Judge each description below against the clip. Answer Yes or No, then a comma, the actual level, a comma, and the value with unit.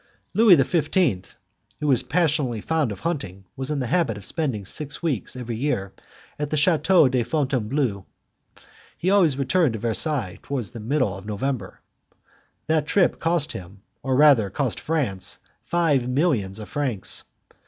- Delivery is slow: No, average, 155 wpm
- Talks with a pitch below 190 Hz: Yes, low, 135 Hz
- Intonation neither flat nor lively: No, wide, 6.1 semitones